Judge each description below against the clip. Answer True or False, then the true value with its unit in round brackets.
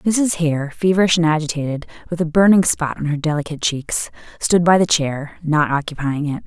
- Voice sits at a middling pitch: True (160 Hz)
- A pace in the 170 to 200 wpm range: True (185 wpm)